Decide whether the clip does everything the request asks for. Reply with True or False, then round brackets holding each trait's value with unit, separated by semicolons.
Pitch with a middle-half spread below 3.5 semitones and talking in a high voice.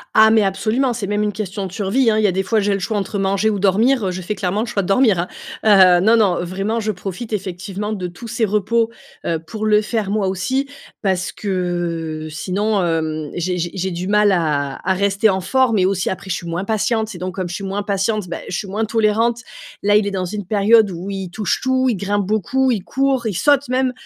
True (2.9 semitones; 200 Hz)